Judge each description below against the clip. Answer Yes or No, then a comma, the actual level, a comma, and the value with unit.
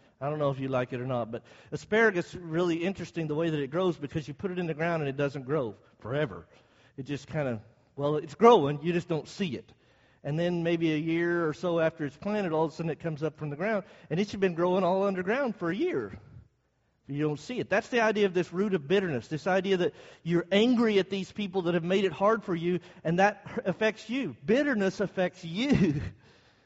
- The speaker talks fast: Yes, fast, 240 wpm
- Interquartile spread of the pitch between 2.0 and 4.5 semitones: No, average, 4.9 semitones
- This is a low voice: No, medium, 170 Hz